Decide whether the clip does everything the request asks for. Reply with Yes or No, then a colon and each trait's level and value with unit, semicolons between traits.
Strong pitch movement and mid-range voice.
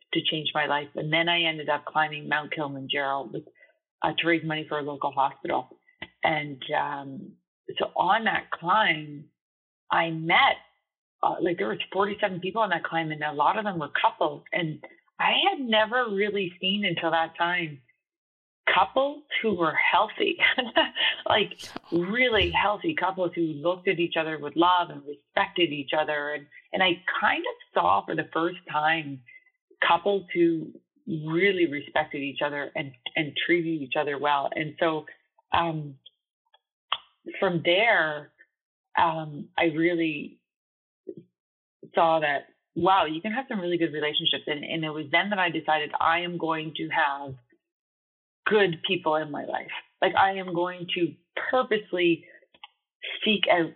No: average, 4.3 semitones; medium, 165 Hz